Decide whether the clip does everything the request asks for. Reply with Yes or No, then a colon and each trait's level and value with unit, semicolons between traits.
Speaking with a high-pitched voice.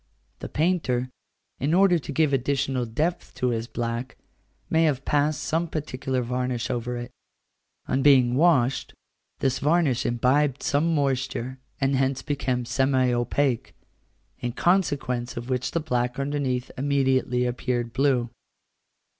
No: low, 130 Hz